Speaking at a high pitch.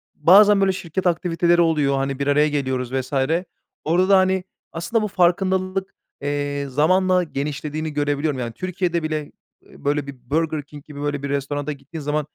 No: medium, 150 Hz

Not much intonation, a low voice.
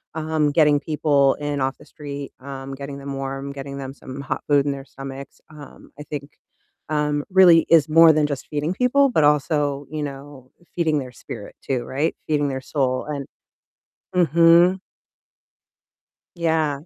No: narrow, 2.1 semitones; medium, 145 Hz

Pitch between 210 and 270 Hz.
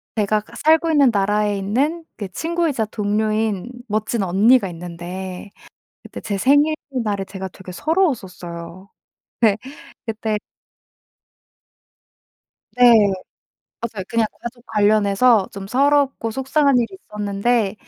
Yes: high, 215 Hz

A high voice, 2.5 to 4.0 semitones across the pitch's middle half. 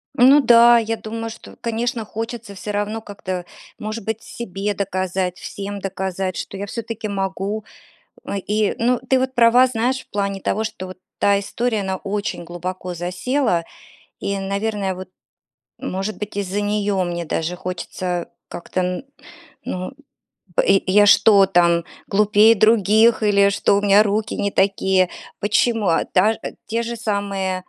Yes: high, 200 Hz; average, 2.9 semitones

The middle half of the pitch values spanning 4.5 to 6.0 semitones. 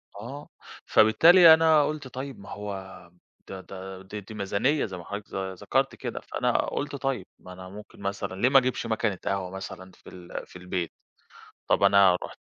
Yes: wide, 5.4 semitones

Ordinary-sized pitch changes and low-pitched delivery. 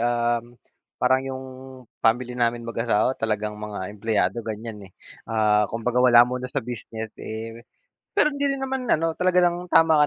Yes: average, 3.5 semitones; low, 120 Hz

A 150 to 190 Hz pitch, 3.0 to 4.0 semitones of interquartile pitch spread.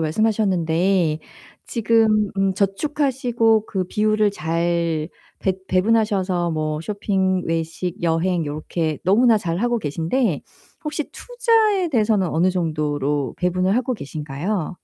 No: medium, 185 Hz; average, 5.1 semitones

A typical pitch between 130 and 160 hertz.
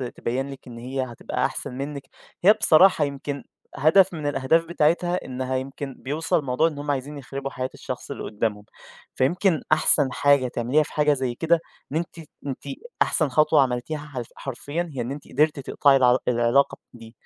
Yes: medium, 140 Hz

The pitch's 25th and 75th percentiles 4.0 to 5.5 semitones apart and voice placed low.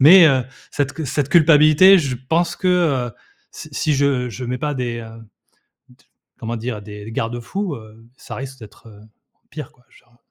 Yes: average, 4.5 semitones; low, 130 Hz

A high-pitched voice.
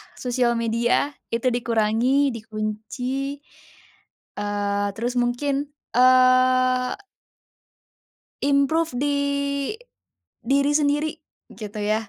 Yes: very high, 250 Hz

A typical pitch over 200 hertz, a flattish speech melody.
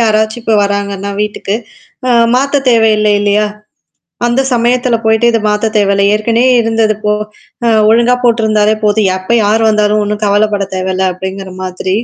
Yes: high, 215 Hz; narrow, 2.0 semitones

